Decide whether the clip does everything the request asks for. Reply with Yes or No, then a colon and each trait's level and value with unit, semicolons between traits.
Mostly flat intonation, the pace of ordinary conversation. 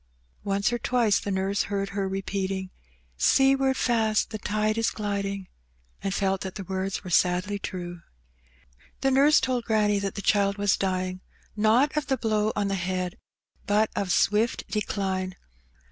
Yes: narrow, 2.2 semitones; average, 160 wpm